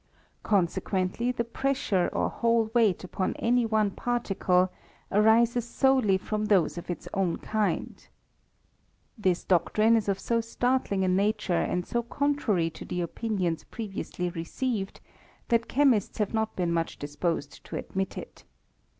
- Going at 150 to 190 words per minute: No, average, 140 wpm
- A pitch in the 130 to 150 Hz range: No, high, 210 Hz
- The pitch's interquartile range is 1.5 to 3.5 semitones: No, average, 4.2 semitones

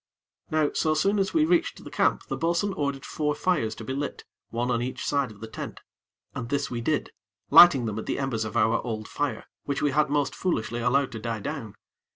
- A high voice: No, medium, 140 Hz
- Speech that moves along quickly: Yes, fast, 220 wpm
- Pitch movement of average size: Yes, average, 4.9 semitones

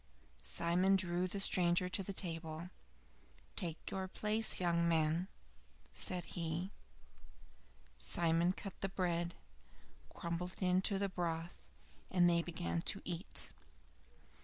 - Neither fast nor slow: No, slow, 115 wpm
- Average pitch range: No, narrow, 1.8 semitones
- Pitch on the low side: No, medium, 175 Hz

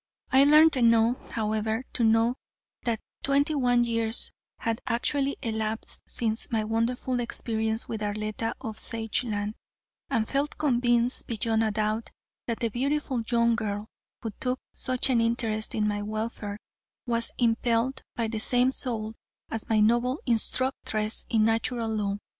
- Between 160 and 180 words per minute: No, average, 140 wpm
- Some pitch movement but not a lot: No, narrow, 2.0 semitones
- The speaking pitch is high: Yes, high, 230 Hz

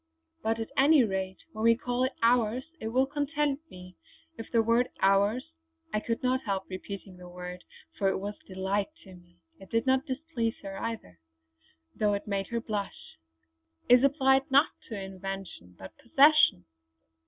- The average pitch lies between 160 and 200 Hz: No, high, 220 Hz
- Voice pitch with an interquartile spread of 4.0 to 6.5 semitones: Yes, average, 5.1 semitones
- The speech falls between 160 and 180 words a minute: Yes, average, 170 wpm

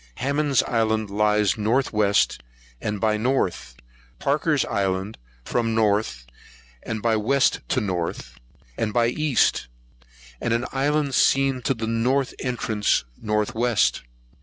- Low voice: Yes, low, 110 Hz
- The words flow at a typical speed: No, slow, 125 wpm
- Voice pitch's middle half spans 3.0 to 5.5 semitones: Yes, average, 3.7 semitones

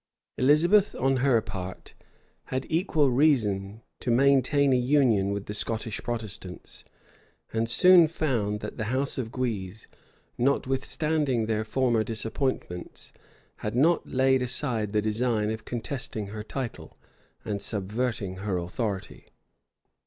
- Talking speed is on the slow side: Yes, slow, 125 wpm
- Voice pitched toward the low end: Yes, low, 120 Hz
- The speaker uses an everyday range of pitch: Yes, average, 4.1 semitones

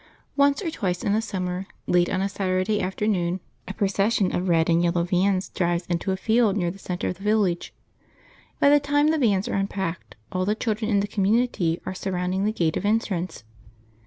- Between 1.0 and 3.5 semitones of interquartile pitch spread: Yes, average, 3.0 semitones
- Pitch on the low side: No, high, 195 Hz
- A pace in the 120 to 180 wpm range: No, average, 200 wpm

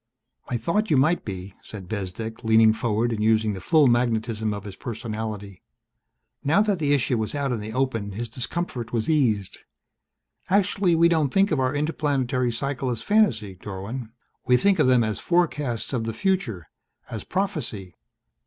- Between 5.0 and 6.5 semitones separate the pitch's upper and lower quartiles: Yes, wide, 5.5 semitones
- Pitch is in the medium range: No, low, 120 Hz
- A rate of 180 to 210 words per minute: No, average, 170 wpm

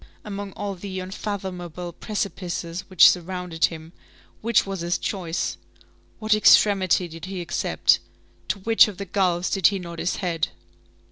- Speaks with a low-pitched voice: No, medium, 185 Hz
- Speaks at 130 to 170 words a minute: Yes, average, 145 wpm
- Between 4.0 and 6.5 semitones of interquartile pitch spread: No, narrow, 2.4 semitones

